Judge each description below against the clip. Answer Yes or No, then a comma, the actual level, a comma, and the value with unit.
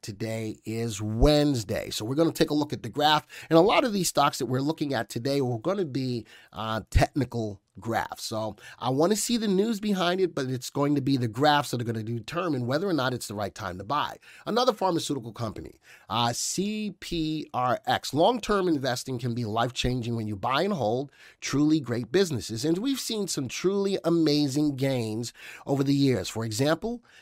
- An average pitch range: No, wide, 5.8 semitones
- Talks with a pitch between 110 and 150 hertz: Yes, medium, 140 Hz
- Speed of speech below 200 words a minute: No, fast, 205 wpm